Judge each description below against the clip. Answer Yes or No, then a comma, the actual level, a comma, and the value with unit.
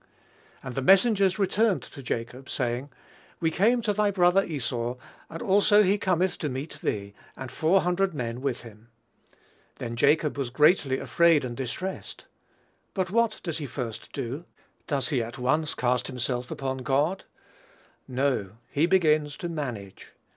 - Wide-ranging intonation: Yes, wide, 6.6 semitones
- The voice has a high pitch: No, medium, 145 Hz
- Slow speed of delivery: No, average, 155 wpm